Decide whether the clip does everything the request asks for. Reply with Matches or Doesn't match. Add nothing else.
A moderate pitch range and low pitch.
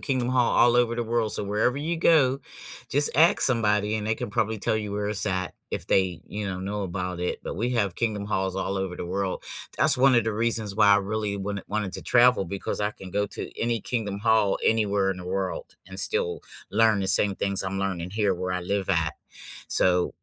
Matches